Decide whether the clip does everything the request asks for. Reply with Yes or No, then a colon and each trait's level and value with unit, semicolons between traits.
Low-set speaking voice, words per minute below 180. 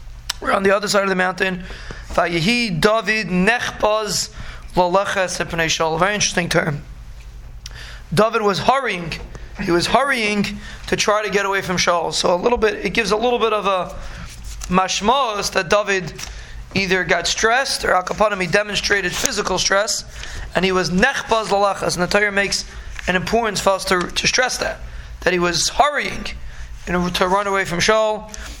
No: high, 190 Hz; average, 145 wpm